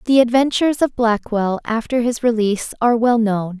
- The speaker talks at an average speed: Yes, average, 165 wpm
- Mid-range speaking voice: No, high, 230 Hz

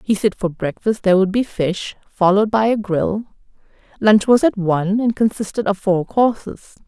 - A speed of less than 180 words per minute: No, average, 185 wpm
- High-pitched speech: Yes, high, 205 Hz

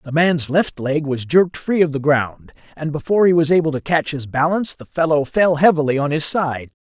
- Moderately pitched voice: Yes, medium, 155 Hz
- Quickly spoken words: Yes, fast, 230 wpm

